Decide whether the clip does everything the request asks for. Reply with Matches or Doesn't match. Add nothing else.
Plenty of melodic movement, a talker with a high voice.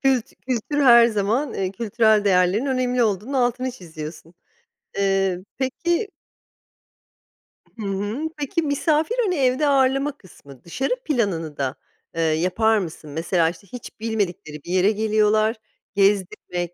Matches